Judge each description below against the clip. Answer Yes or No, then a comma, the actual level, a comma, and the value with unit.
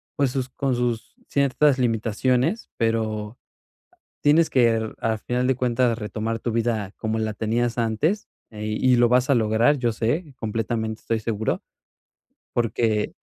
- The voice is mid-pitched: No, low, 115 Hz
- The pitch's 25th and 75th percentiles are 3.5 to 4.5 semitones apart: No, narrow, 2.4 semitones